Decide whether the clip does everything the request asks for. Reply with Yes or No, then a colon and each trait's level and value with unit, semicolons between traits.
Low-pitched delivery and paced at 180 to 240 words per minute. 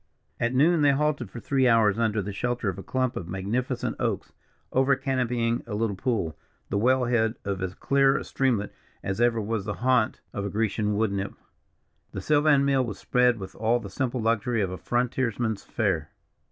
Yes: low, 115 Hz; average, 190 wpm